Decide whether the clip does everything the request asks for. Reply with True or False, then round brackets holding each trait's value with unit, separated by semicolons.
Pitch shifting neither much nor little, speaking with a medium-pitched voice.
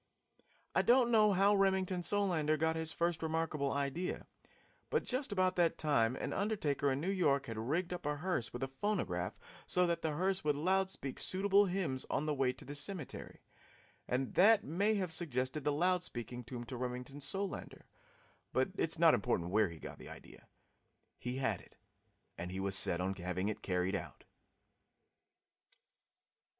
False (6.6 semitones; 155 Hz)